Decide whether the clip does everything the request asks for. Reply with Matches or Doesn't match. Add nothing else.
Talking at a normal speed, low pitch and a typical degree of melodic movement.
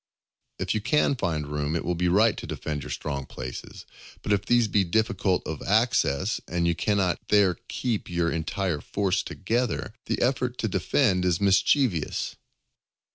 Matches